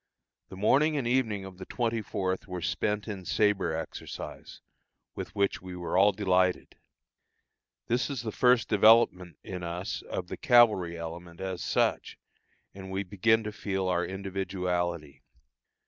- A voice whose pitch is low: Yes, very low, 95 Hz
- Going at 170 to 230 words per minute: No, average, 145 wpm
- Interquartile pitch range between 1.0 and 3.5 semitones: Yes, average, 3.1 semitones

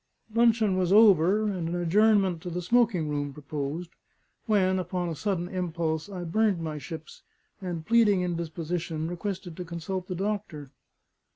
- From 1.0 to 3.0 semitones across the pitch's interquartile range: No, average, 3.5 semitones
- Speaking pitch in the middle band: Yes, medium, 180 Hz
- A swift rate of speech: No, average, 150 wpm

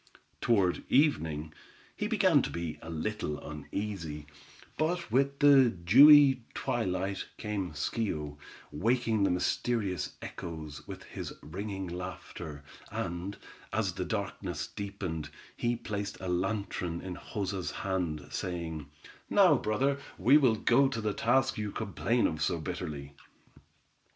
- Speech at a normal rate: No, slow, 125 wpm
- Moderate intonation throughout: No, wide, 5.8 semitones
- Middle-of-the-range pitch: No, low, 100 Hz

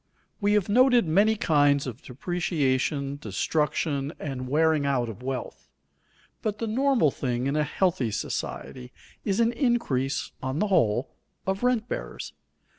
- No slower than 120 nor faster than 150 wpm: Yes, average, 145 wpm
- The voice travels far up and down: Yes, wide, 7.6 semitones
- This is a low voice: No, medium, 150 Hz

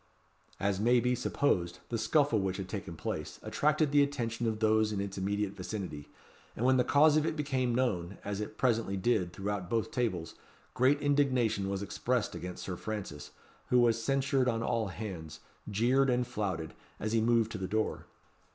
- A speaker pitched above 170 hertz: No, low, 110 Hz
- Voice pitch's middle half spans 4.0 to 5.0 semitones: Yes, average, 4.3 semitones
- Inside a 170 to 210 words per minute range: Yes, average, 180 wpm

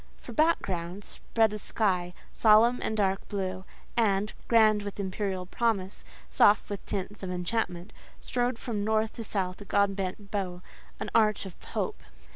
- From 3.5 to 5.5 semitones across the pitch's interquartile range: No, average, 2.7 semitones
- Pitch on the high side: Yes, high, 205 Hz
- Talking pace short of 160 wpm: Yes, average, 145 wpm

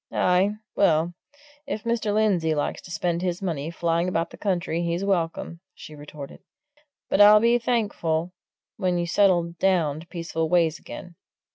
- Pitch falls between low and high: Yes, medium, 175 Hz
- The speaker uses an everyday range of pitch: Yes, average, 3.1 semitones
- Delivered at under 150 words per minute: No, average, 155 wpm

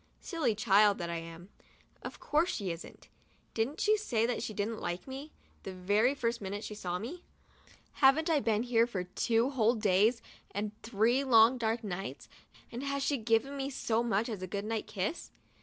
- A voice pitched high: Yes, high, 225 Hz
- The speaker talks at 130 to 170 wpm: No, average, 195 wpm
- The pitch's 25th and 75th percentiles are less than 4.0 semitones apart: No, average, 4.3 semitones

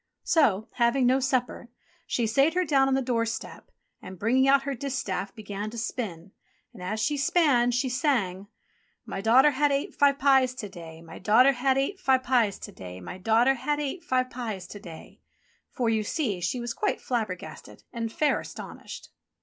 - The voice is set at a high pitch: Yes, high, 245 Hz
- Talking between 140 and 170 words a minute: No, average, 180 wpm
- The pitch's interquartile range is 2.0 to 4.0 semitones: No, average, 4.5 semitones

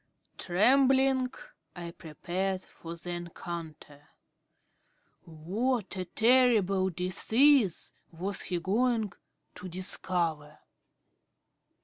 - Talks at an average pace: No, slow, 70 wpm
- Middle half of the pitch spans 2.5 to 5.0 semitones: No, wide, 5.5 semitones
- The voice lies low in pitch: No, medium, 185 Hz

